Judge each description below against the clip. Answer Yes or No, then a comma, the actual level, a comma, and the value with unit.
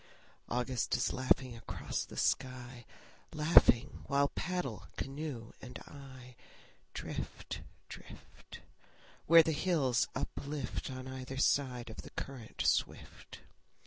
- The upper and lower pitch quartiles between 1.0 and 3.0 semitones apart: Yes, narrow, 2.5 semitones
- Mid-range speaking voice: No, low, 130 Hz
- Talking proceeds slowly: Yes, slow, 110 wpm